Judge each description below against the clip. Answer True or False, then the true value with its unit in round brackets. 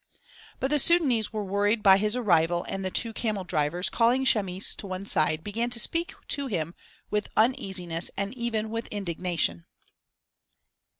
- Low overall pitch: False (205 Hz)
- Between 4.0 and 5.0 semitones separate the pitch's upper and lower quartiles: True (4.4 semitones)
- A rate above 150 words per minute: True (160 wpm)